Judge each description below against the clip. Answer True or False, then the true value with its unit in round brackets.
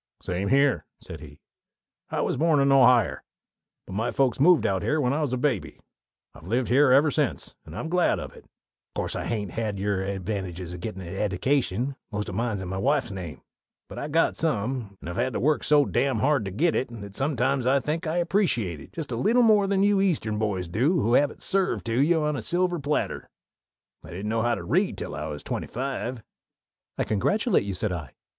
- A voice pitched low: True (125 Hz)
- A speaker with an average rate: False (220 wpm)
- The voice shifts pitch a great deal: True (7.2 semitones)